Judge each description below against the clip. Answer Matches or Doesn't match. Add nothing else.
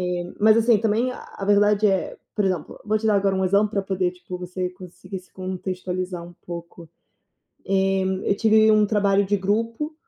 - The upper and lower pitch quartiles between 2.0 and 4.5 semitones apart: Matches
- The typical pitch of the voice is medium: Doesn't match